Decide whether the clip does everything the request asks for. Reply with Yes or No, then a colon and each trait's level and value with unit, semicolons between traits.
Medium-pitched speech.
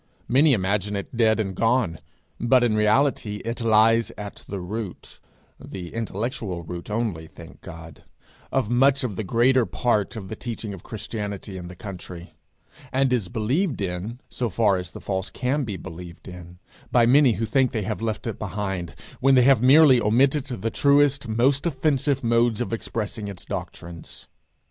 No: low, 110 Hz